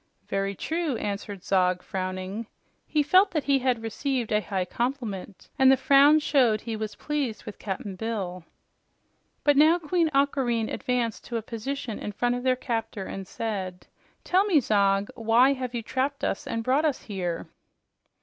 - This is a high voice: Yes, high, 230 Hz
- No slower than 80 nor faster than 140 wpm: No, average, 170 wpm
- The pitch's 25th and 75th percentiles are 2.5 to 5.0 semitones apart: No, wide, 5.4 semitones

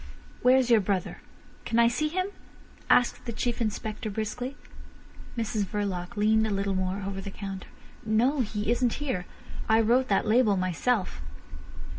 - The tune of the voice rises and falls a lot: No, average, 3.5 semitones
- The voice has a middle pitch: No, high, 220 Hz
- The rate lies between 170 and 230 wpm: No, average, 150 wpm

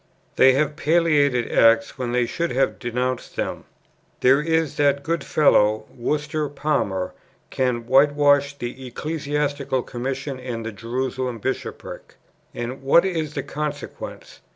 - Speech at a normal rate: No, slow, 130 wpm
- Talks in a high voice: No, low, 135 Hz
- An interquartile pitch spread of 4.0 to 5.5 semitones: No, average, 3.3 semitones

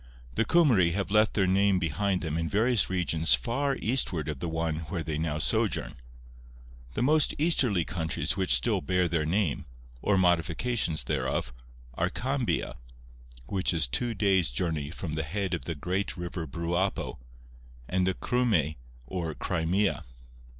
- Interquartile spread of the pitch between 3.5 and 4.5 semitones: Yes, average, 4.1 semitones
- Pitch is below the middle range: Yes, very low, 90 Hz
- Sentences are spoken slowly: No, average, 150 wpm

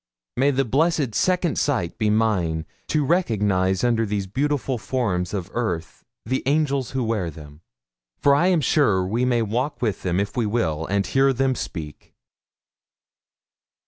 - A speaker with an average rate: Yes, average, 155 wpm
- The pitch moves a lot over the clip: Yes, wide, 6.2 semitones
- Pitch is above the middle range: No, low, 115 Hz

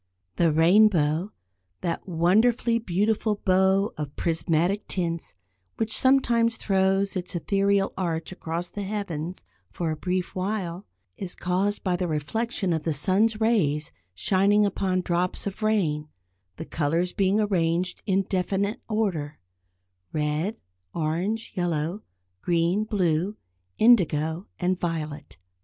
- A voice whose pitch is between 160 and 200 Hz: Yes, medium, 185 Hz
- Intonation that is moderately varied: Yes, average, 3.7 semitones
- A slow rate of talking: Yes, slow, 120 wpm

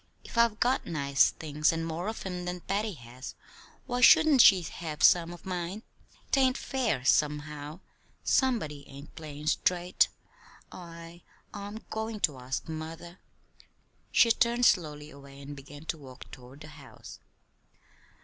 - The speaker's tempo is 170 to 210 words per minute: No, average, 145 wpm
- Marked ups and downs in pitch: Yes, wide, 5.7 semitones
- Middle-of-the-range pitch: Yes, medium, 165 Hz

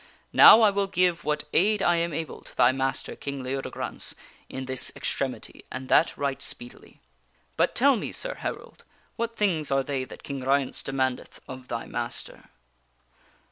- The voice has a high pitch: No, medium, 140 Hz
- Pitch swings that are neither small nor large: No, wide, 5.7 semitones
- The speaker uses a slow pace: No, average, 165 wpm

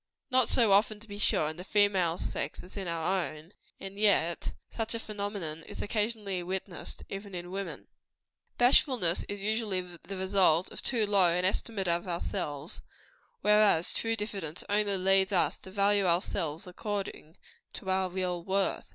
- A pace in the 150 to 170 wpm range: Yes, average, 160 wpm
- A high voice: Yes, high, 195 Hz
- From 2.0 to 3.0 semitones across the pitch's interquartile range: Yes, average, 2.7 semitones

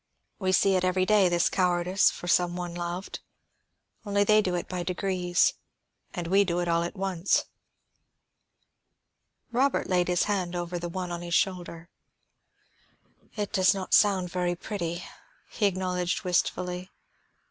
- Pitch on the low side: No, medium, 180 Hz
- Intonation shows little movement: Yes, narrow, 1.6 semitones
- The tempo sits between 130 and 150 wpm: Yes, average, 145 wpm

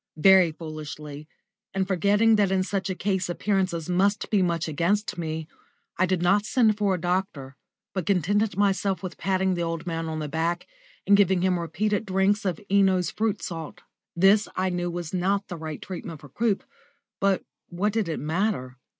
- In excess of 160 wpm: Yes, average, 180 wpm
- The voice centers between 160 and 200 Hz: Yes, medium, 185 Hz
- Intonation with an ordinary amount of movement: Yes, average, 3.1 semitones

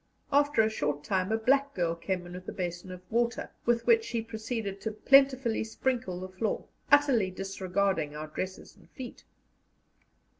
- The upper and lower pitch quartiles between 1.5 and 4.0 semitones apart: No, average, 4.7 semitones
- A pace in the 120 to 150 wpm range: No, average, 165 wpm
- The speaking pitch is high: Yes, high, 215 Hz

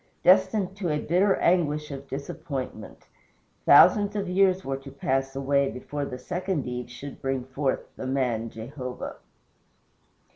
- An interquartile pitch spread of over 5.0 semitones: Yes, wide, 5.4 semitones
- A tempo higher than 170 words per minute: No, average, 140 wpm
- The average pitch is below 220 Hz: Yes, medium, 140 Hz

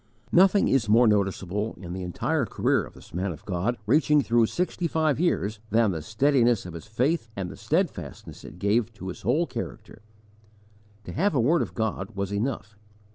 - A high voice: No, low, 110 Hz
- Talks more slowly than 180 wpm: No, average, 185 wpm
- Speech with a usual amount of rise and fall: No, wide, 5.8 semitones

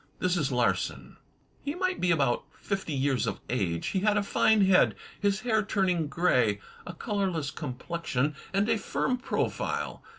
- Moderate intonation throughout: No, wide, 6.7 semitones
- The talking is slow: No, average, 160 wpm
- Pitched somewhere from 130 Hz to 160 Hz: No, medium, 180 Hz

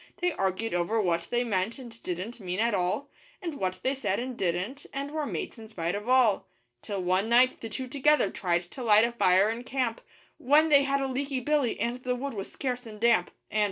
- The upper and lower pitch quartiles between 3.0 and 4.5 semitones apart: No, average, 5.3 semitones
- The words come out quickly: Yes, fast, 225 wpm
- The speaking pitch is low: No, high, 235 Hz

